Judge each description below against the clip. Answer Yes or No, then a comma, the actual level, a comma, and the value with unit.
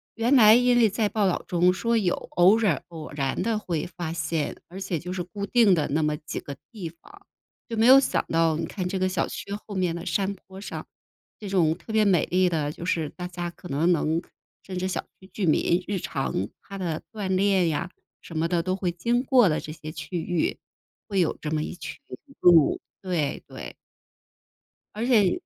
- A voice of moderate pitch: Yes, medium, 180 Hz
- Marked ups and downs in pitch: No, average, 3.7 semitones